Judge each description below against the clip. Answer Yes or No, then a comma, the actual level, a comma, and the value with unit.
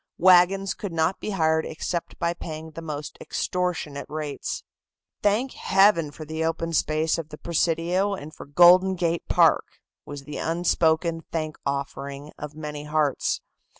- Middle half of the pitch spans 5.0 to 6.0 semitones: No, narrow, 2.6 semitones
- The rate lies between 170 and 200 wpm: No, average, 150 wpm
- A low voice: No, medium, 160 Hz